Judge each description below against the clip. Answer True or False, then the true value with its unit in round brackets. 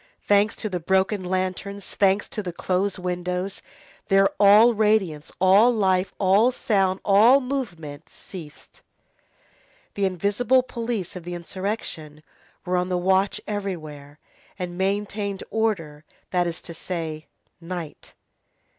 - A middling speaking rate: False (125 wpm)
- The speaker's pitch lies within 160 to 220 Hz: True (190 Hz)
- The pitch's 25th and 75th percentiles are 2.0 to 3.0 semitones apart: True (2.6 semitones)